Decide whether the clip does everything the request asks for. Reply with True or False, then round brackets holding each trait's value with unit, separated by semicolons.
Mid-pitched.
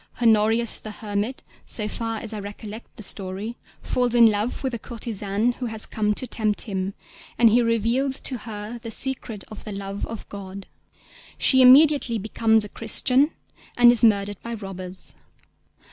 False (220 Hz)